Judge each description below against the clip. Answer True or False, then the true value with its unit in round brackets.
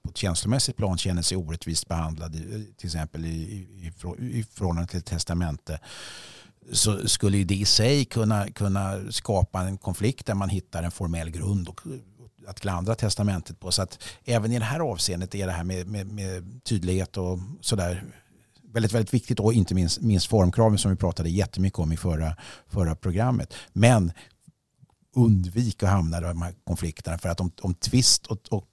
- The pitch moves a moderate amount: True (4.0 semitones)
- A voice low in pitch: True (95 Hz)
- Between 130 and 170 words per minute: False (180 wpm)